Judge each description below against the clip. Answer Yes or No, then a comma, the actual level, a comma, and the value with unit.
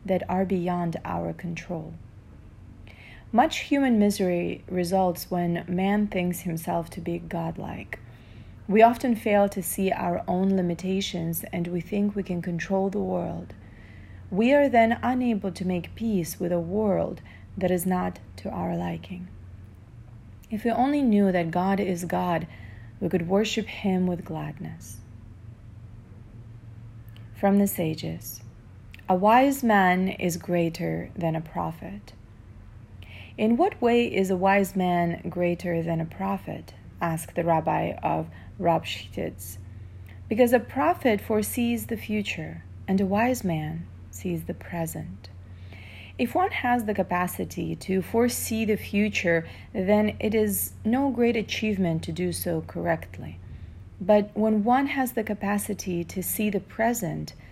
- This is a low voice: No, medium, 175 Hz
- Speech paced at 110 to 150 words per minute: Yes, slow, 135 wpm